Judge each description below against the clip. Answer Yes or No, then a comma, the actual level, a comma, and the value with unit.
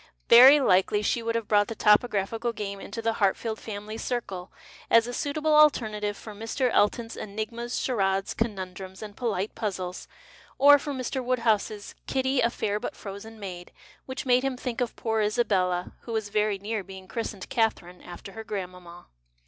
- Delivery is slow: No, average, 175 wpm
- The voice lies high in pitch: Yes, high, 220 Hz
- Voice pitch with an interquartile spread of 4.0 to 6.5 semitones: No, average, 3.3 semitones